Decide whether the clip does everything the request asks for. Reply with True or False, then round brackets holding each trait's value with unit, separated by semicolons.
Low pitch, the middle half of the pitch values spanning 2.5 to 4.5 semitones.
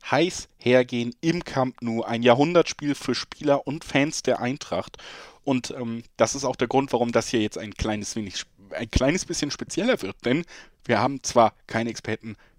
True (125 Hz; 3.1 semitones)